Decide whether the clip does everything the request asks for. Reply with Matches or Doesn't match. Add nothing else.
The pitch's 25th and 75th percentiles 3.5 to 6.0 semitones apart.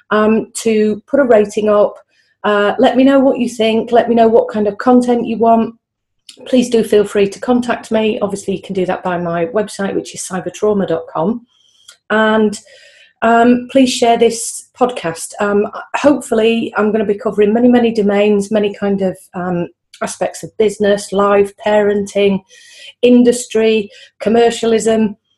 Doesn't match